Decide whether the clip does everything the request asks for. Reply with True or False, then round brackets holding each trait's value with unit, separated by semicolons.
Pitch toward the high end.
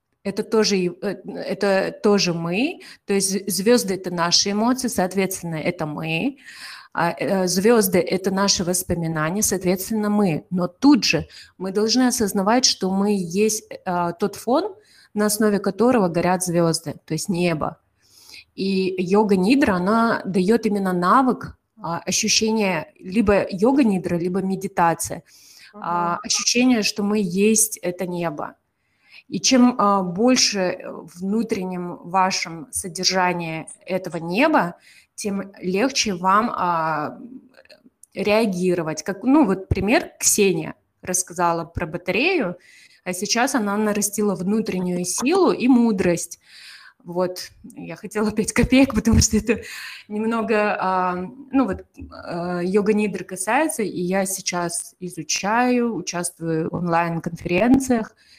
True (195 Hz)